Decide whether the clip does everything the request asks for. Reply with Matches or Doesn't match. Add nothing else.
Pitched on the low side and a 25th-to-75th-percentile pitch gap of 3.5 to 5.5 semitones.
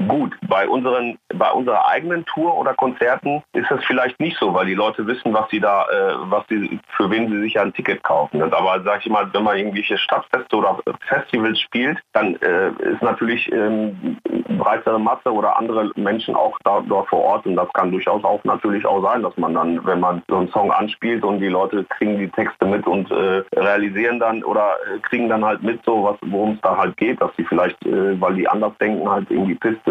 Doesn't match